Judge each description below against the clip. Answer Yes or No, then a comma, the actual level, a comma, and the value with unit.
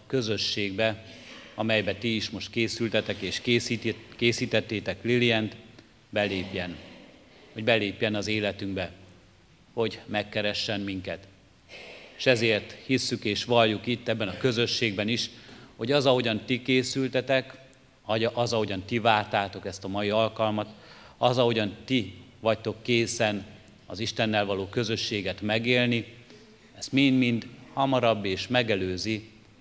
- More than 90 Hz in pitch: Yes, low, 110 Hz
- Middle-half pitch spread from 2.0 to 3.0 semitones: Yes, average, 2.7 semitones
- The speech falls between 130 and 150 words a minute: No, average, 115 wpm